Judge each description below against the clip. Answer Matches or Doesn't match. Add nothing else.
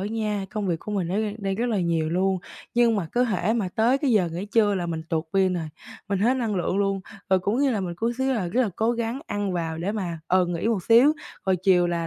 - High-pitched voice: Matches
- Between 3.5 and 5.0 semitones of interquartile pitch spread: Matches